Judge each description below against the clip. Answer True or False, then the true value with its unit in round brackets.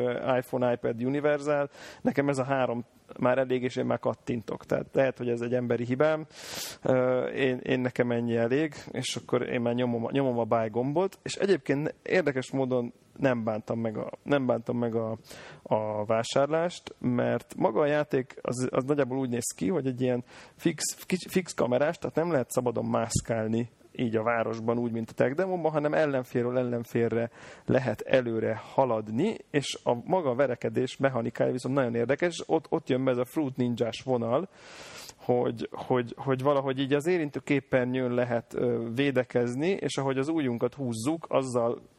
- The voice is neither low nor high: False (125 Hz)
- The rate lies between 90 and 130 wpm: False (165 wpm)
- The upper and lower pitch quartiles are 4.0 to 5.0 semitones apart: False (2.9 semitones)